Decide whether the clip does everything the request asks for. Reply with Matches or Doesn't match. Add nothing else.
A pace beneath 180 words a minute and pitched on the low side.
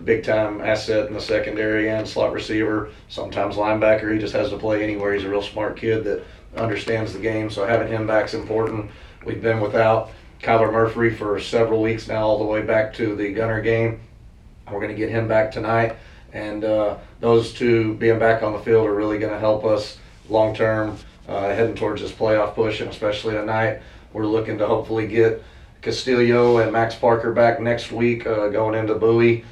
Doesn't match